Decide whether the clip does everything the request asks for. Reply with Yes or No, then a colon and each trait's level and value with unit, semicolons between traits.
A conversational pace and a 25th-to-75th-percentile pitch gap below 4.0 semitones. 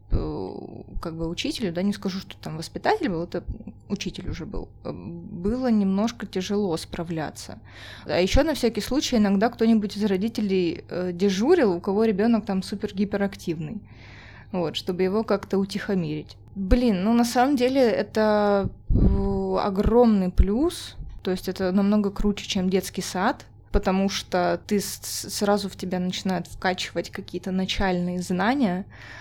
Yes: average, 135 wpm; average, 3.1 semitones